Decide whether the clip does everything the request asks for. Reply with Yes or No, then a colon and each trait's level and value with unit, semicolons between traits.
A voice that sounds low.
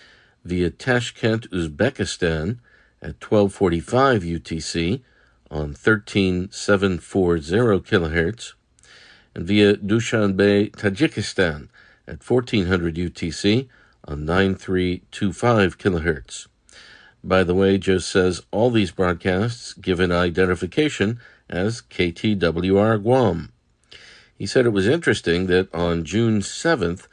Yes: very low, 95 Hz